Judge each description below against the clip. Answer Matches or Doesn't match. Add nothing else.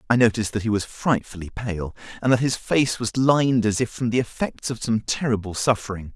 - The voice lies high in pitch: Doesn't match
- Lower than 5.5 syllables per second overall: Doesn't match